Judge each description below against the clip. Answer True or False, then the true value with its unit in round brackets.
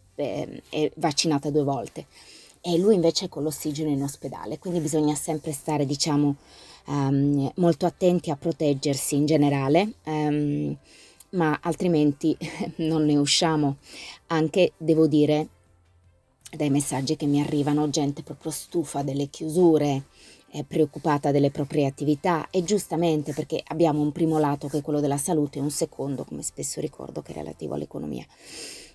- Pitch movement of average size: False (2.2 semitones)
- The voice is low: False (150 Hz)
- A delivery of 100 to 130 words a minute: False (145 wpm)